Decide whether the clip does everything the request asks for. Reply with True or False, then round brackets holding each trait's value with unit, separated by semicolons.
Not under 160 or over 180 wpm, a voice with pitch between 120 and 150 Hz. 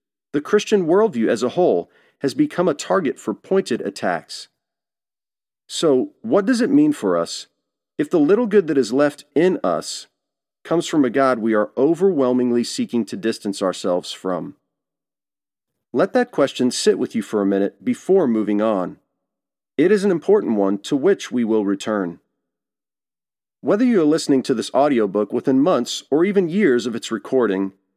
True (165 wpm; 135 Hz)